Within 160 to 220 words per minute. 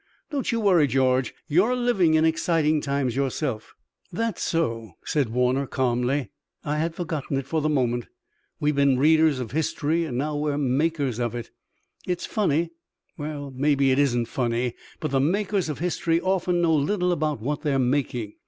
Yes: average, 170 wpm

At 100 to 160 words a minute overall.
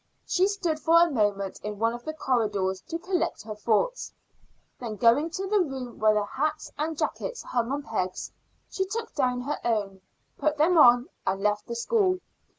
No: average, 185 wpm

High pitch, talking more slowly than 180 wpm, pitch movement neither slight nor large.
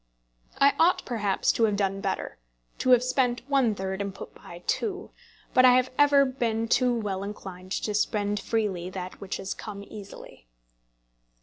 Yes: high, 210 Hz; average, 170 wpm; average, 4.5 semitones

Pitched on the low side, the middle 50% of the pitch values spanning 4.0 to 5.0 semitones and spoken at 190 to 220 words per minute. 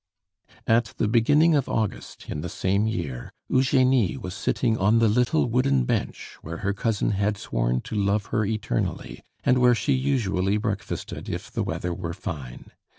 No: low, 105 Hz; average, 4.7 semitones; average, 165 wpm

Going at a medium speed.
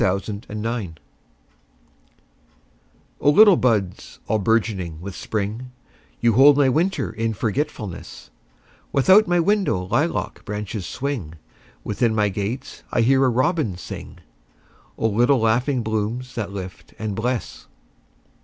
No: slow, 115 wpm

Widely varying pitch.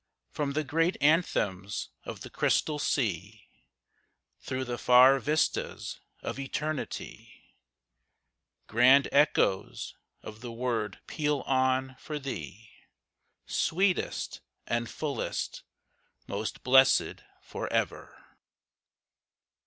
No: average, 4.4 semitones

